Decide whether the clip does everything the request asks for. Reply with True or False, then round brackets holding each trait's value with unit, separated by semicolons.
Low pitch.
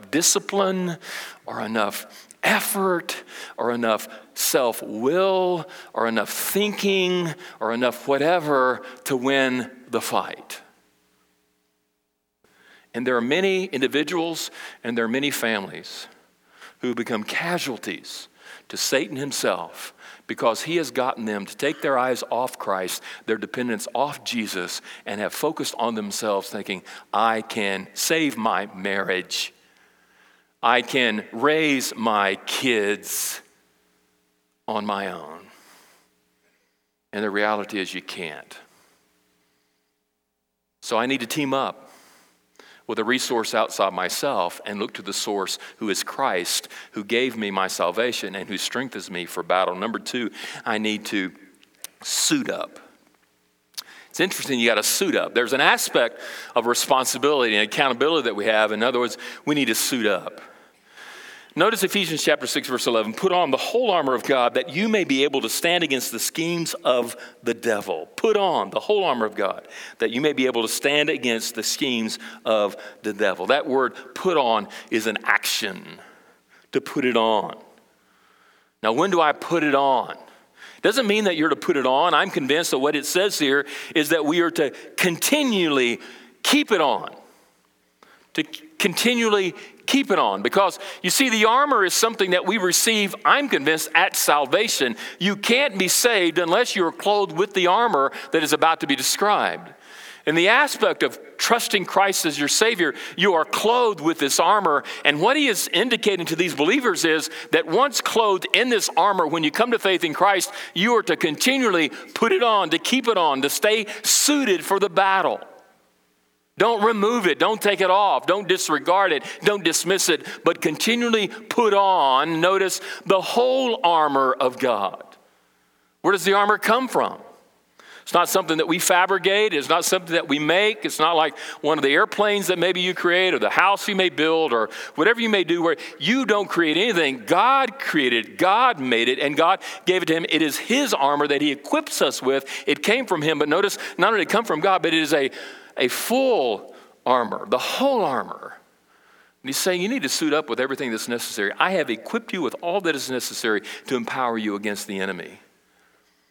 False (160 Hz)